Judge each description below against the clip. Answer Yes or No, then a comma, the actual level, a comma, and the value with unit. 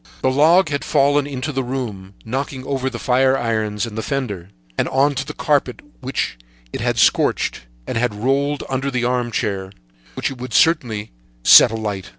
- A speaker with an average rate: Yes, average, 175 wpm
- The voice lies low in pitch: Yes, low, 130 Hz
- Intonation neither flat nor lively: Yes, average, 3.8 semitones